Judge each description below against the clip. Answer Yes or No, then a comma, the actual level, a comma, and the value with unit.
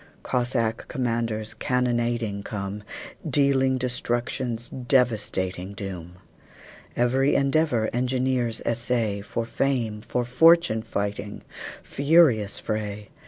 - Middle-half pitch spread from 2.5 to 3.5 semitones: Yes, average, 3.2 semitones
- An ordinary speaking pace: No, slow, 85 wpm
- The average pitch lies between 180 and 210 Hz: No, low, 120 Hz